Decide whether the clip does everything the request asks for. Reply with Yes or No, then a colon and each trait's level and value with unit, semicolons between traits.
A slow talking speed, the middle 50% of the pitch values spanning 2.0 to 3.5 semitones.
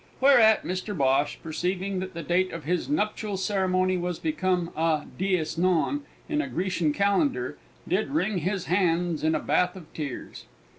No: average, 160 wpm; average, 3.1 semitones